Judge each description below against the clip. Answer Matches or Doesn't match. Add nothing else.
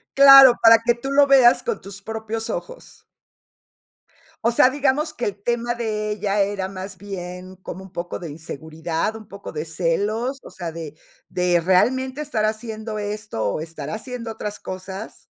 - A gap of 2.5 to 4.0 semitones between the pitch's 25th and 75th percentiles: Doesn't match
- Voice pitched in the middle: Doesn't match